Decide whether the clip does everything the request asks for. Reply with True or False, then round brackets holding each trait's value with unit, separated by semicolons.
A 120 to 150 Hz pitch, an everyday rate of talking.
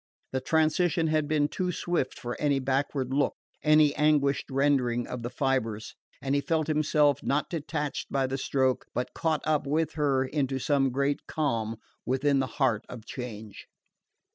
True (140 Hz; 165 wpm)